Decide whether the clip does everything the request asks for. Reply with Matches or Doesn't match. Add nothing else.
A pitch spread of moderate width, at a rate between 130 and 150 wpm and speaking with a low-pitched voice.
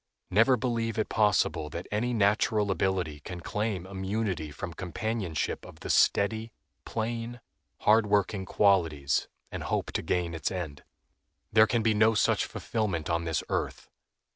Matches